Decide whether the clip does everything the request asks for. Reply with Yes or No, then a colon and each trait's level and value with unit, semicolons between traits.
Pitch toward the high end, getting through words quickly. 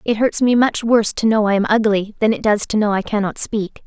Yes: high, 215 Hz; fast, 280 wpm